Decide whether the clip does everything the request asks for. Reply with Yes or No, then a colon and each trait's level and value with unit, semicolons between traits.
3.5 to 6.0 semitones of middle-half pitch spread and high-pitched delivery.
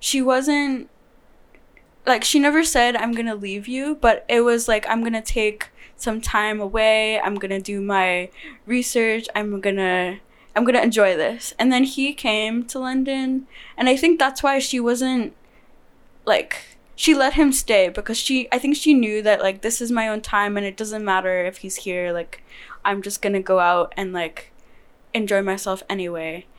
Yes: average, 4.5 semitones; high, 220 Hz